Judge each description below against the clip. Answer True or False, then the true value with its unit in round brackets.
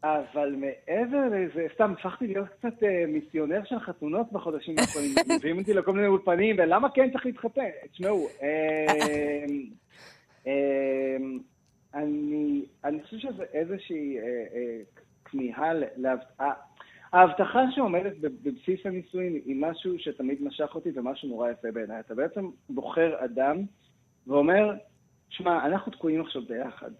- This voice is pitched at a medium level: True (160 Hz)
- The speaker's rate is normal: True (110 wpm)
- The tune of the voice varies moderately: False (5.9 semitones)